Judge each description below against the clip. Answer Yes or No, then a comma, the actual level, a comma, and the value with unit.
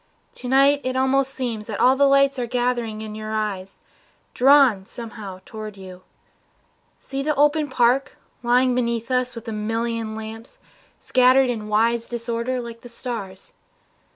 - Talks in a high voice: Yes, high, 235 Hz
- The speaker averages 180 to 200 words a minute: No, average, 155 wpm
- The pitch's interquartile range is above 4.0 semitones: No, average, 3.0 semitones